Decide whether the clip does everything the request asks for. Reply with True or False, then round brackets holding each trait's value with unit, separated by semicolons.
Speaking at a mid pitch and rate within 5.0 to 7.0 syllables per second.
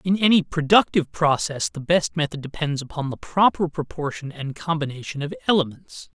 True (150 Hz; 5.5 syllables/s)